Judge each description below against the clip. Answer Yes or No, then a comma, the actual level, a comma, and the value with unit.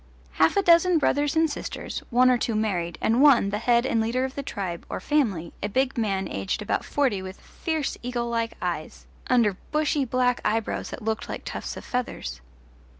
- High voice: Yes, high, 235 Hz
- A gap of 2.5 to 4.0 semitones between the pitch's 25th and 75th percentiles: No, average, 4.8 semitones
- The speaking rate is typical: Yes, average, 195 wpm